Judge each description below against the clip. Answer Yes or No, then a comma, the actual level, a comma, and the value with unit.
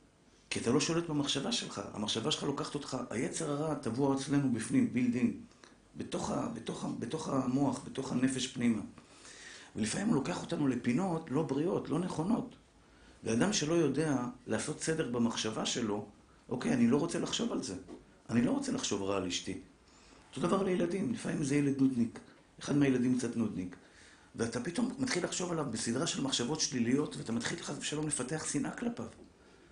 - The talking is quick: Yes, fast, 160 wpm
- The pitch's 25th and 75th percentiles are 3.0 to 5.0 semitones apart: No, wide, 5.6 semitones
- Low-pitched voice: No, medium, 145 Hz